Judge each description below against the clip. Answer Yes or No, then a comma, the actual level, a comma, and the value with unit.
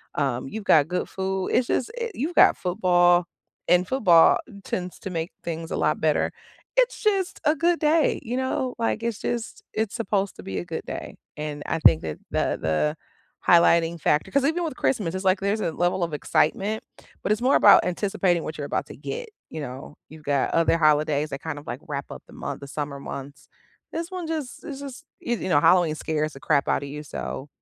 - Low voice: No, medium, 175 Hz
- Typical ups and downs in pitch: No, wide, 7.7 semitones